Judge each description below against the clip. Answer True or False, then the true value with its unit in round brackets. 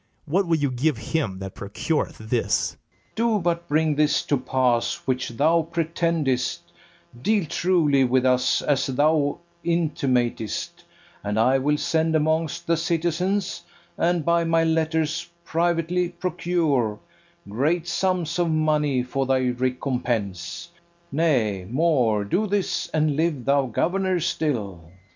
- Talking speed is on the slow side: True (130 wpm)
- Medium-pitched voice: True (155 Hz)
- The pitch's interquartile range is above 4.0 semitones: True (4.9 semitones)